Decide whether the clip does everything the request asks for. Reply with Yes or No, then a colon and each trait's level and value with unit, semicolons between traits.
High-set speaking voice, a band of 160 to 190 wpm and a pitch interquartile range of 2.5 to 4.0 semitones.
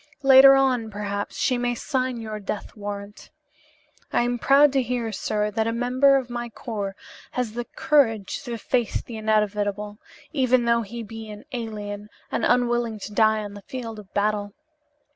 Yes: high, 225 Hz; average, 170 wpm; average, 2.8 semitones